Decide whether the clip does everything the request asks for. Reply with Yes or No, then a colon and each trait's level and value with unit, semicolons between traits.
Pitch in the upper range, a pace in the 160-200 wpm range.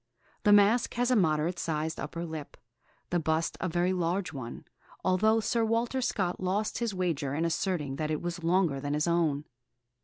No: medium, 175 Hz; average, 180 wpm